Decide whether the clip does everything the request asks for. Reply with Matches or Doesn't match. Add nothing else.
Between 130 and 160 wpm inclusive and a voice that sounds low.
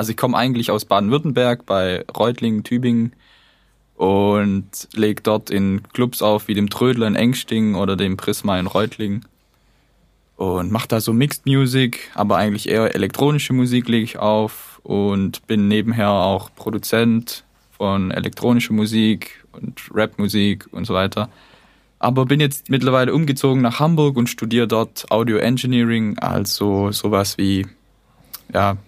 Matches